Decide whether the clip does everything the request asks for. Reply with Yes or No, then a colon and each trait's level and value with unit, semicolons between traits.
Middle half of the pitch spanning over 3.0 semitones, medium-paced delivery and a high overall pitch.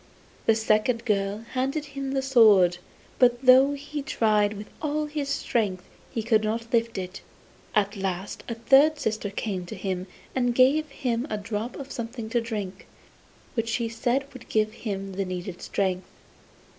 Yes: average, 4.4 semitones; average, 165 wpm; high, 225 Hz